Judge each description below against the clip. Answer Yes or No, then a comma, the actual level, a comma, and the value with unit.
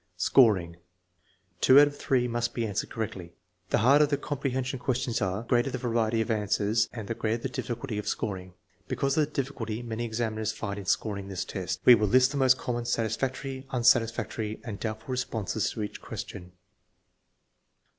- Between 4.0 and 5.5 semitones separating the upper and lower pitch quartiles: No, average, 3.3 semitones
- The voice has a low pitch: Yes, low, 115 Hz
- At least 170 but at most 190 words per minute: Yes, average, 175 wpm